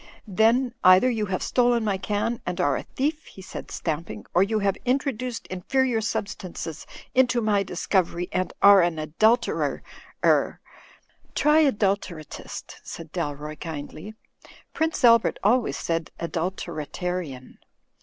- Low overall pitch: No, high, 195 Hz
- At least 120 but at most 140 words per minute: Yes, slow, 135 wpm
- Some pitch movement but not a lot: No, wide, 5.8 semitones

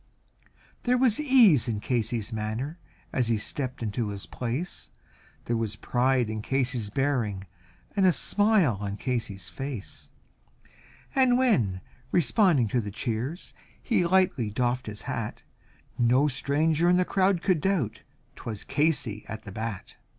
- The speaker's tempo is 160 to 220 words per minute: No, average, 140 wpm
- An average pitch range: No, wide, 7.9 semitones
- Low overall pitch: Yes, low, 125 Hz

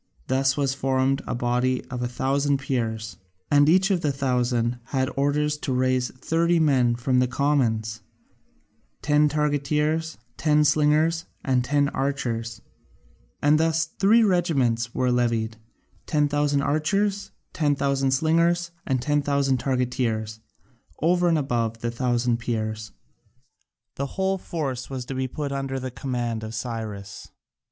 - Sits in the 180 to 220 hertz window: No, low, 135 Hz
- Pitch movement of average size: Yes, average, 3.5 semitones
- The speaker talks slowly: Yes, slow, 130 wpm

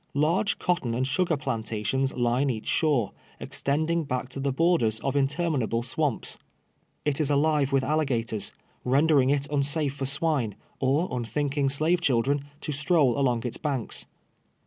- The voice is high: No, medium, 140 Hz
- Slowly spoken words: No, average, 145 wpm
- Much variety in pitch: No, average, 3.2 semitones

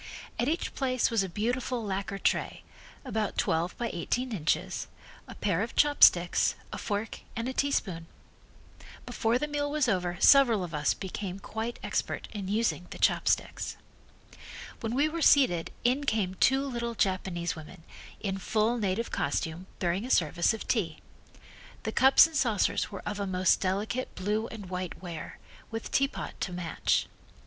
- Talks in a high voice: Yes, high, 210 Hz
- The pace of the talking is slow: No, average, 160 wpm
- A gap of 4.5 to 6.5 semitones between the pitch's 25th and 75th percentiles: Yes, average, 5.0 semitones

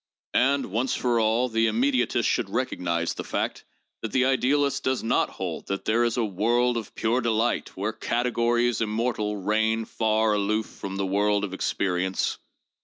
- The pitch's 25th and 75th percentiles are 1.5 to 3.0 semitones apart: Yes, narrow, 2.6 semitones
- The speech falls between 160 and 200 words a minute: Yes, average, 170 wpm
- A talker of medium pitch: No, low, 110 Hz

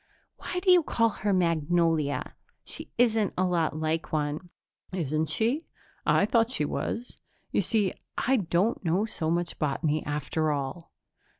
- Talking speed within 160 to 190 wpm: No, average, 145 wpm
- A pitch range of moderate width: No, wide, 5.9 semitones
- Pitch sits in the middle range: Yes, medium, 170 Hz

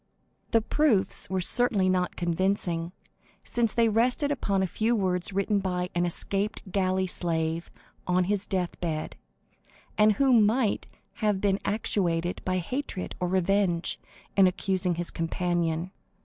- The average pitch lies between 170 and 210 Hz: Yes, high, 190 Hz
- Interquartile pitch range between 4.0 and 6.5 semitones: No, average, 3.0 semitones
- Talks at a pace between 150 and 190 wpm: No, slow, 135 wpm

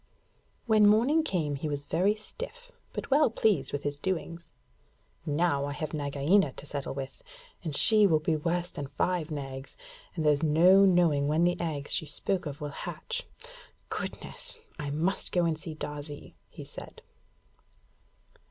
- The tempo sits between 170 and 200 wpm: No, average, 160 wpm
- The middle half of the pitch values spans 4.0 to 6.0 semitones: Yes, average, 4.6 semitones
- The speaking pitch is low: No, medium, 160 Hz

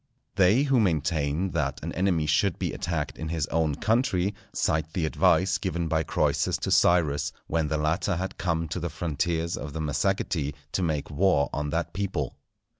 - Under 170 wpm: No, average, 180 wpm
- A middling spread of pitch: Yes, average, 3.3 semitones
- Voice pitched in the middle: No, very low, 80 Hz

